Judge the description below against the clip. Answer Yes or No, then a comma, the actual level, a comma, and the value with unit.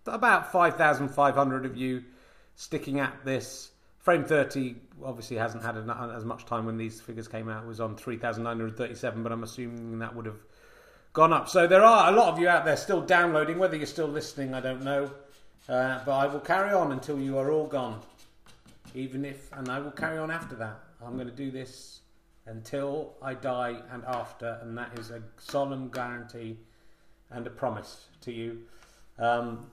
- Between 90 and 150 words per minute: No, average, 190 wpm